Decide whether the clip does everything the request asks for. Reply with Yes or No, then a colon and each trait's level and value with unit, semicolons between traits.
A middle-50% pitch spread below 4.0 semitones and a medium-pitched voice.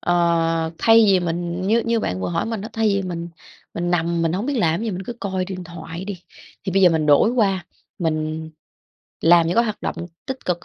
Yes: average, 3.6 semitones; medium, 175 Hz